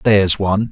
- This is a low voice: Yes, low, 100 Hz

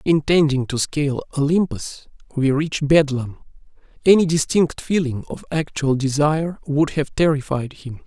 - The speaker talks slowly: Yes, slow, 125 wpm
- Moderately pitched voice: Yes, medium, 145 Hz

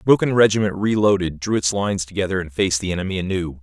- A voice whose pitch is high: No, very low, 95 Hz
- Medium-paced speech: No, fast, 215 wpm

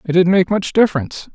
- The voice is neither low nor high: Yes, medium, 180 Hz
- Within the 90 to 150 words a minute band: No, fast, 225 wpm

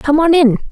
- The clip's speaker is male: No, female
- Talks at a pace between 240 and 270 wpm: Yes, fast, 250 wpm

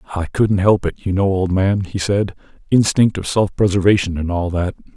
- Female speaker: No, male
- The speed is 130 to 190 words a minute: No, fast, 205 wpm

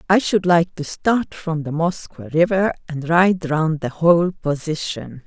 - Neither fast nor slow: Yes, average, 170 wpm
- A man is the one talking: No, female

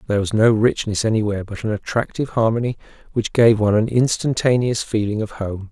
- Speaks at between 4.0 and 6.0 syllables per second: No, 6.2 syllables/s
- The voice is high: No, low, 110 Hz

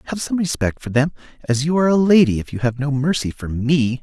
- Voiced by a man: Yes, male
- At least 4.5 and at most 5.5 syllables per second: No, 6.0 syllables/s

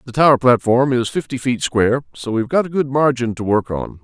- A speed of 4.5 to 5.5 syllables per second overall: No, 5.8 syllables/s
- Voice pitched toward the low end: Yes, low, 125 Hz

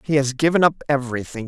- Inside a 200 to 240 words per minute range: Yes, fast, 205 wpm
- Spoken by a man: Yes, male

